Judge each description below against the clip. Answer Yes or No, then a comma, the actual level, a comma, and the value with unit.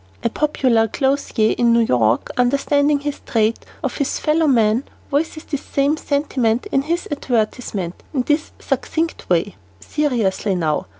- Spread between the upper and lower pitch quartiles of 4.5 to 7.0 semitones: Yes, average, 4.9 semitones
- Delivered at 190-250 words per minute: No, average, 145 wpm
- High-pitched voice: Yes, very high, 255 Hz